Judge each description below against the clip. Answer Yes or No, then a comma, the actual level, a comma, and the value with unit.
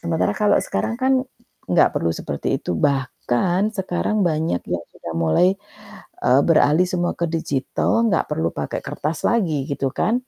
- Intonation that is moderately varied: No, wide, 6.3 semitones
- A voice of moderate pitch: Yes, medium, 165 Hz